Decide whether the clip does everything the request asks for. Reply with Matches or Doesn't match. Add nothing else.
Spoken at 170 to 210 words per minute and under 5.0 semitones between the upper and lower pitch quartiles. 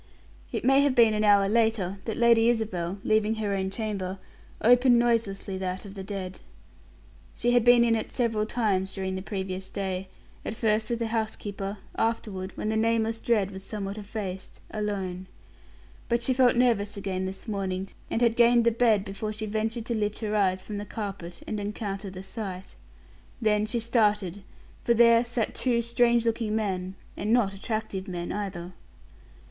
Matches